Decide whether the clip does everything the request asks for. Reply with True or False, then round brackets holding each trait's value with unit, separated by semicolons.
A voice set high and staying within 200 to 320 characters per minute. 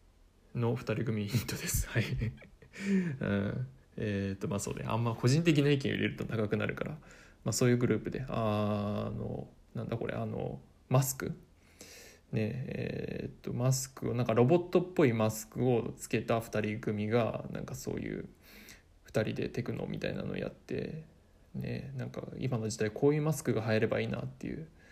False (115 Hz; 315 characters per minute)